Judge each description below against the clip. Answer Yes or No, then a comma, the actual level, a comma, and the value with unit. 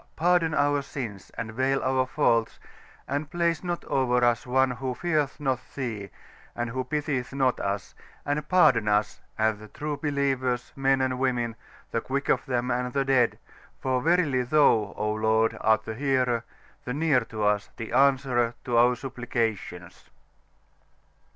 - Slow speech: No, average, 155 wpm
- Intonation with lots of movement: No, average, 3.3 semitones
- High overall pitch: No, low, 130 Hz